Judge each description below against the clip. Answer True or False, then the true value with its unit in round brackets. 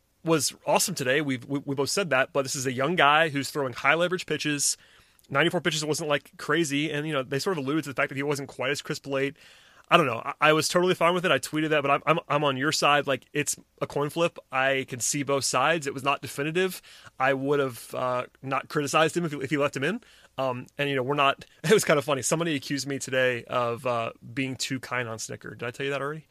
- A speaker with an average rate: False (270 wpm)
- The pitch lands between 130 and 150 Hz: True (140 Hz)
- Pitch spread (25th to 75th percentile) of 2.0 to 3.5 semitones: True (2.6 semitones)